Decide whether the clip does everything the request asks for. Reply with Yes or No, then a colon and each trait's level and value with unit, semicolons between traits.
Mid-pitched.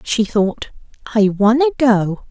No: high, 225 Hz